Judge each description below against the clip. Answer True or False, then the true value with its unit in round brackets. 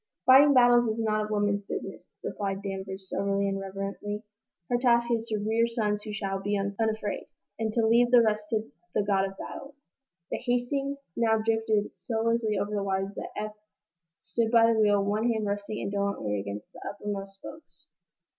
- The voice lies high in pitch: True (210 Hz)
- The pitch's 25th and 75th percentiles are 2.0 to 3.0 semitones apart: True (2.5 semitones)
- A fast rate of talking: False (180 wpm)